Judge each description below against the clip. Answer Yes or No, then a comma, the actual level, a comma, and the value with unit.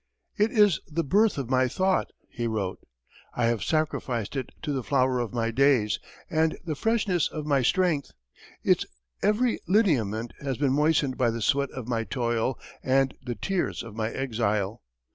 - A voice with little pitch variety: No, average, 5.3 semitones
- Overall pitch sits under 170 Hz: Yes, low, 135 Hz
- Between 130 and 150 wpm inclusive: No, average, 170 wpm